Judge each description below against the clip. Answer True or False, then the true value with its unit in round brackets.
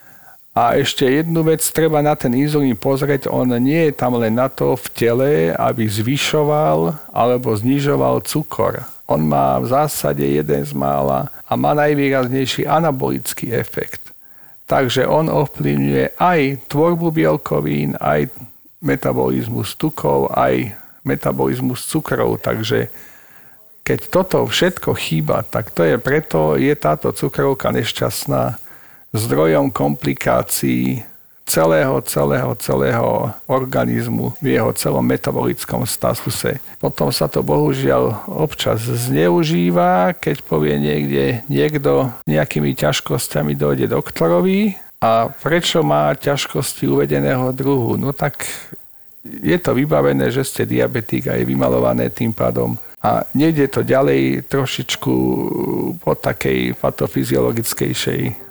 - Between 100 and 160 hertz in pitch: False (75 Hz)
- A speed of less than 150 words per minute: True (115 wpm)